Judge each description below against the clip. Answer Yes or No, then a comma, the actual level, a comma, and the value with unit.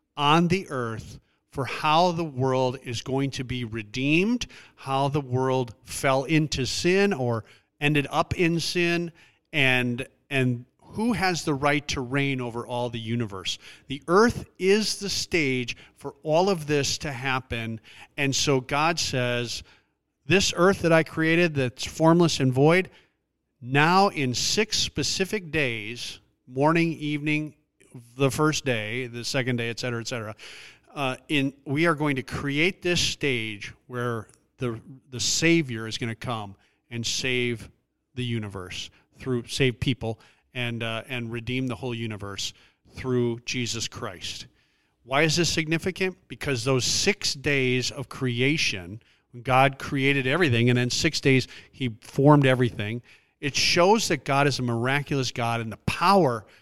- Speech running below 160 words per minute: Yes, average, 150 wpm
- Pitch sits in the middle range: No, low, 130 Hz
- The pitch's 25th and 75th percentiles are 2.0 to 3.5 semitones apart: No, average, 4.2 semitones